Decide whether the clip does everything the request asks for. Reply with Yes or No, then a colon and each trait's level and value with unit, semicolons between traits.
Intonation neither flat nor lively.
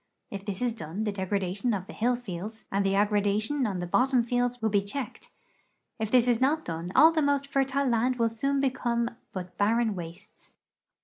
Yes: average, 4.1 semitones